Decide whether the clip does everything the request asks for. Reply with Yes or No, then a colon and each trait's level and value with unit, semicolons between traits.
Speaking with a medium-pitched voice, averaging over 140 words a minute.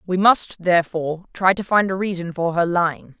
Yes: medium, 180 Hz; fast, 205 wpm